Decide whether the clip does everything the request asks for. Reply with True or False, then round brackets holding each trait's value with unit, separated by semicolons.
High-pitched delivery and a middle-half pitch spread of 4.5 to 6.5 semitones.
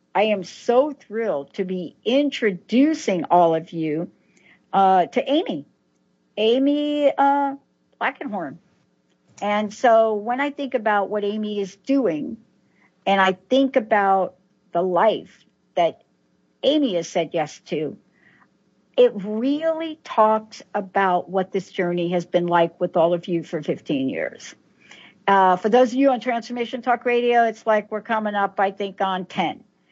True (210 Hz; 5.4 semitones)